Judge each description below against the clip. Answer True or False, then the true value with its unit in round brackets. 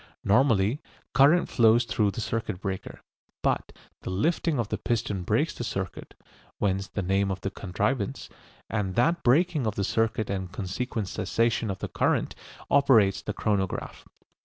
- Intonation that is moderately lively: True (3.7 semitones)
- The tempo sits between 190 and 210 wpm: False (155 wpm)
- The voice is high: False (105 Hz)